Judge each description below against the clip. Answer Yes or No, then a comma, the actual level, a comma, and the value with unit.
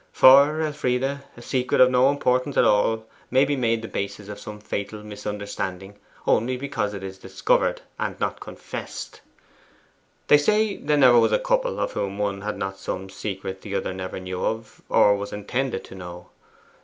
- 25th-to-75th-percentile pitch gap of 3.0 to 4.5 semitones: No, average, 5.2 semitones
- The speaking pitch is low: Yes, low, 105 Hz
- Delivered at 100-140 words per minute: No, average, 175 wpm